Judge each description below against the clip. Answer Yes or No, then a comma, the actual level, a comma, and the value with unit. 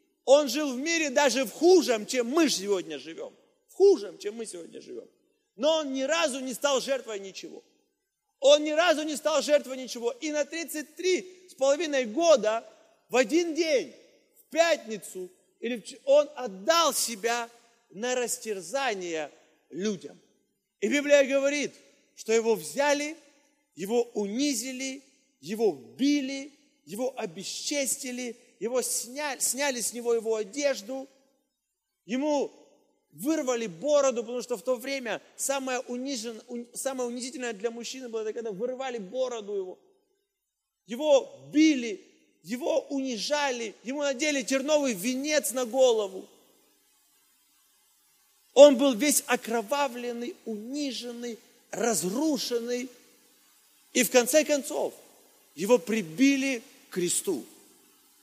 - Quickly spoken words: No, average, 115 wpm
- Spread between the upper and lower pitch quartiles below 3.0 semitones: No, average, 3.8 semitones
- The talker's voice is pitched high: Yes, very high, 265 Hz